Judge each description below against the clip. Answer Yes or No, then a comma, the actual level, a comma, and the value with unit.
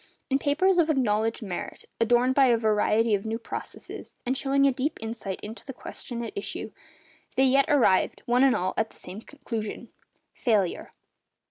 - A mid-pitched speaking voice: No, high, 240 Hz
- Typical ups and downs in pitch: Yes, average, 3.7 semitones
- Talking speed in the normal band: Yes, average, 165 wpm